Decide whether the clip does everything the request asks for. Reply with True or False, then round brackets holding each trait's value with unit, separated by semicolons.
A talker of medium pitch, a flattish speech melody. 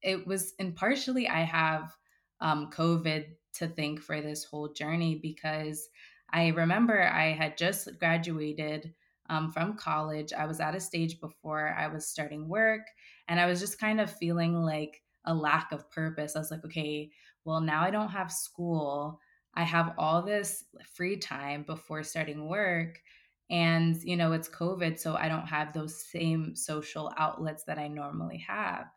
True (160 Hz; 1.9 semitones)